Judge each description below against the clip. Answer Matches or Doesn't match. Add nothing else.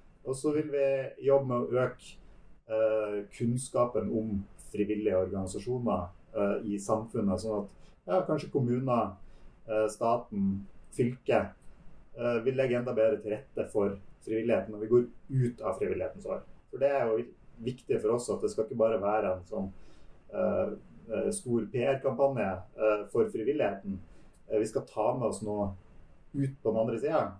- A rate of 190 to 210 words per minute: Doesn't match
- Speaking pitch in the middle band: Doesn't match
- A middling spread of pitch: Matches